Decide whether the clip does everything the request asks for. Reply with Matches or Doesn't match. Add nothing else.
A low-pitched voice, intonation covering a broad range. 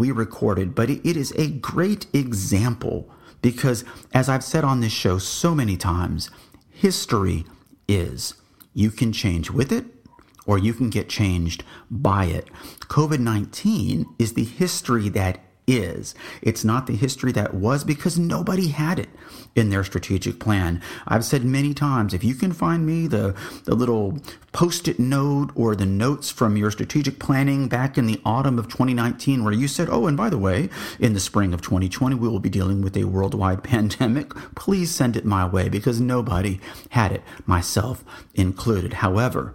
Matches